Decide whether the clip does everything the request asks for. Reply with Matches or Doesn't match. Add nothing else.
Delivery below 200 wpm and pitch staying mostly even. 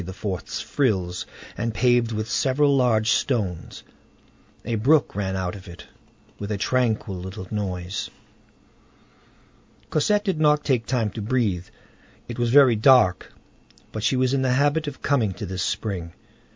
Doesn't match